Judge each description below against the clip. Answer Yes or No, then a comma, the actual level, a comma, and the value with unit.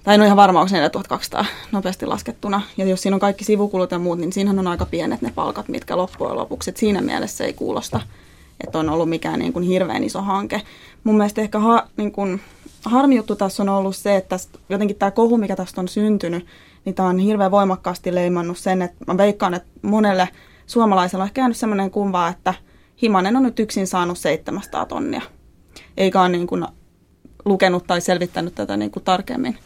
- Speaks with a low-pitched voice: No, high, 195 Hz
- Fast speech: Yes, fast, 200 wpm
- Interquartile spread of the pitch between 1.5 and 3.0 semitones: Yes, narrow, 2.4 semitones